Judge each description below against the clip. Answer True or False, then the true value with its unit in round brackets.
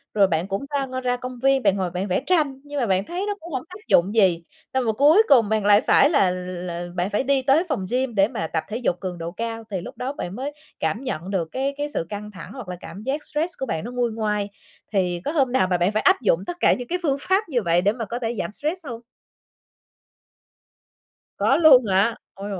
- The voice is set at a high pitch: True (230 Hz)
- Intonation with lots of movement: True (6.2 semitones)